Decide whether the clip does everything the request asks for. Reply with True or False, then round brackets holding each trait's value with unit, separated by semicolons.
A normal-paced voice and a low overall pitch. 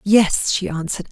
False (160 wpm; 190 Hz)